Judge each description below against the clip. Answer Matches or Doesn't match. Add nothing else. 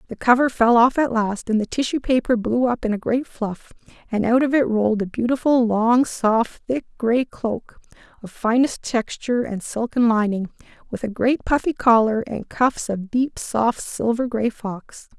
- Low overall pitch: Doesn't match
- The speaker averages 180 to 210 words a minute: Matches